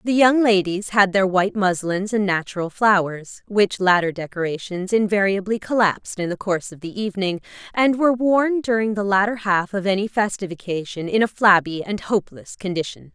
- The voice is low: No, high, 200 Hz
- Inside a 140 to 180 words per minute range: Yes, average, 175 wpm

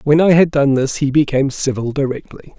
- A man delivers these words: Yes, male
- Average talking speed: No, fast, 210 wpm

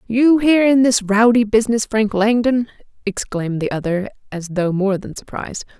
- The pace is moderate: Yes, average, 165 wpm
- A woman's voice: Yes, female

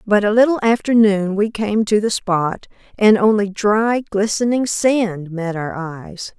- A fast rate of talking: No, average, 170 wpm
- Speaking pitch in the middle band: No, high, 210 Hz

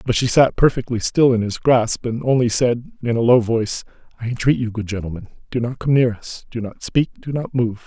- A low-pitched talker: Yes, low, 120 Hz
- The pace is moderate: No, fast, 235 wpm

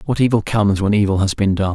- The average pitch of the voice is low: Yes, low, 100 Hz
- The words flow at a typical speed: No, fast, 275 wpm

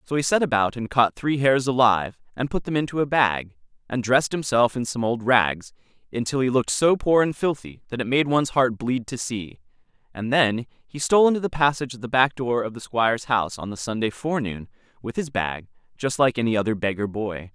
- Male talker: Yes, male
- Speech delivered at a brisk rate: Yes, fast, 220 wpm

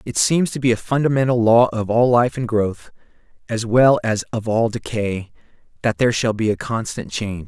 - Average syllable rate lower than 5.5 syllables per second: Yes, 5.1 syllables/s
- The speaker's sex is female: No, male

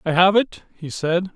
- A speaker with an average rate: No, fast, 220 wpm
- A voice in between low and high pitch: Yes, medium, 180 Hz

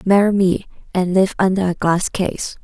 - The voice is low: No, medium, 185 Hz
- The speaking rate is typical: Yes, average, 180 wpm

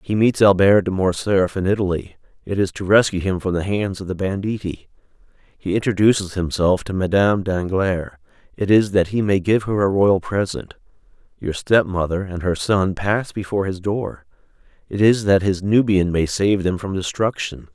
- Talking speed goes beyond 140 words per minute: Yes, average, 170 wpm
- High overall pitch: No, very low, 95 Hz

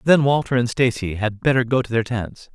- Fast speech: Yes, fast, 235 wpm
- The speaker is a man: Yes, male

